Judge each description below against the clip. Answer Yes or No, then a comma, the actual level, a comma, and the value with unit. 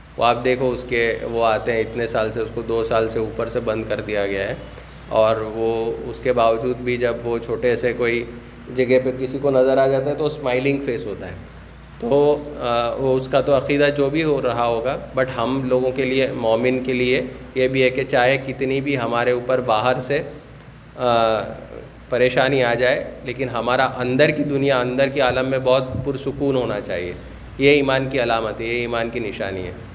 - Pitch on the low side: Yes, low, 125 Hz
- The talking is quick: Yes, fast, 205 wpm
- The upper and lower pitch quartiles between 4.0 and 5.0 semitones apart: No, narrow, 2.5 semitones